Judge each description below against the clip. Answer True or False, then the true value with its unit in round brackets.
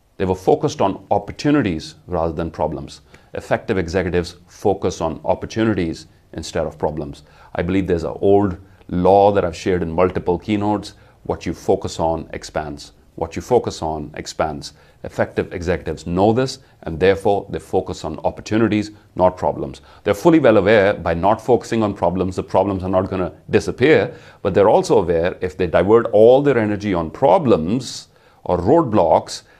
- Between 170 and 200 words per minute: False (160 wpm)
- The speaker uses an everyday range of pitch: True (3.6 semitones)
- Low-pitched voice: True (95 Hz)